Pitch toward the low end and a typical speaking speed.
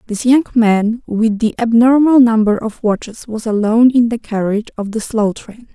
No: high, 225 Hz; average, 190 wpm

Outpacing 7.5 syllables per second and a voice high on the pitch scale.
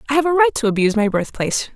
Yes: 7.8 syllables/s; high, 245 Hz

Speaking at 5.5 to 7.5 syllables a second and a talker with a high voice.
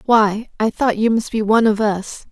No: 4.8 syllables/s; high, 220 Hz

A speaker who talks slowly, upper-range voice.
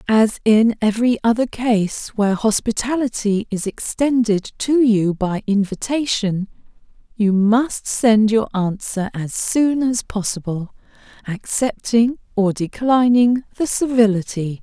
Yes: slow, 110 wpm; high, 220 Hz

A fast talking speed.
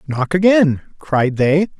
No: slow, 135 wpm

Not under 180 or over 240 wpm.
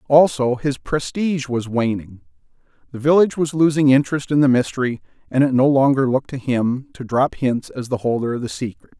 Yes: average, 195 wpm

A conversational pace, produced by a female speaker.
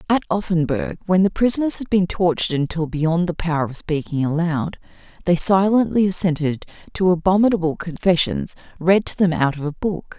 Yes: average, 165 wpm; female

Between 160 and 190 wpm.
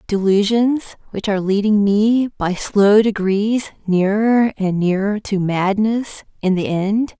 No: slow, 135 wpm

